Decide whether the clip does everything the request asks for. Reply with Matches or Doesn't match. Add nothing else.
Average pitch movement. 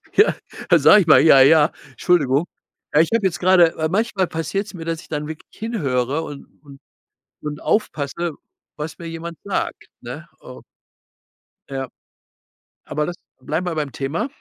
Matches